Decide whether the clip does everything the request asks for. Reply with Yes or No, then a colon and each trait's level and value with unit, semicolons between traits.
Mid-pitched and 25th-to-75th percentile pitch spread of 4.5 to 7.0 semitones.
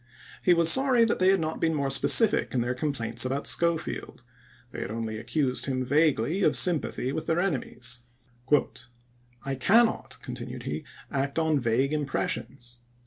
Yes: medium, 145 Hz; average, 4.9 semitones